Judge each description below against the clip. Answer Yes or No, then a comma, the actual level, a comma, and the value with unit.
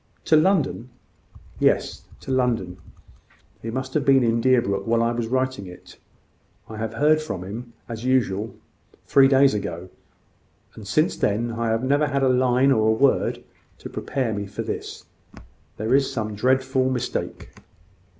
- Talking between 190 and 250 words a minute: No, average, 155 wpm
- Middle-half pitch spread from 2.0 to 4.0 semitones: Yes, average, 3.1 semitones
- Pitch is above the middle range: No, low, 125 Hz